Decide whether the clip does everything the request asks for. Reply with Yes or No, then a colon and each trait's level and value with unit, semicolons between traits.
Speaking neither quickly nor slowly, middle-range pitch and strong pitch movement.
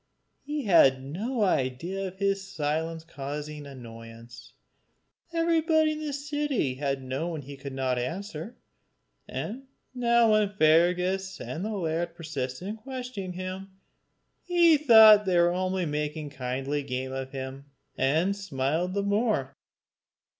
No: slow, 125 wpm; medium, 175 Hz; wide, 7.3 semitones